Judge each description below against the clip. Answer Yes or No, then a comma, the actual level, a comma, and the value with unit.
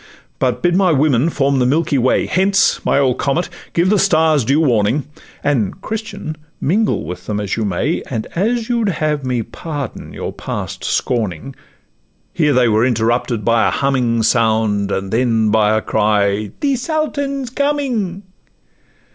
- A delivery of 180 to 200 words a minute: No, average, 165 wpm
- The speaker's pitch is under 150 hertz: Yes, low, 135 Hz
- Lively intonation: Yes, wide, 8.3 semitones